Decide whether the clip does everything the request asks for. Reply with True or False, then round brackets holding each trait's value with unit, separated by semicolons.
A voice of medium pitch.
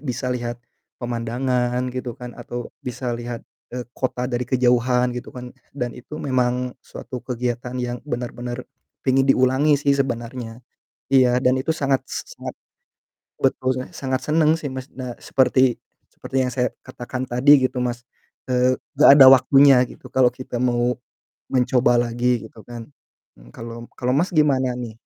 False (125 Hz)